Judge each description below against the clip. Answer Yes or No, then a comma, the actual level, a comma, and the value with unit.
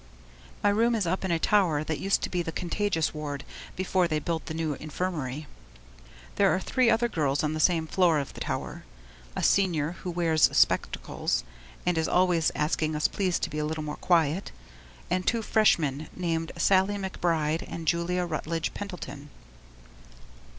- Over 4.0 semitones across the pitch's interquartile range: No, average, 3.2 semitones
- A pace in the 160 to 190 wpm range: Yes, average, 170 wpm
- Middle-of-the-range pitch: Yes, medium, 165 Hz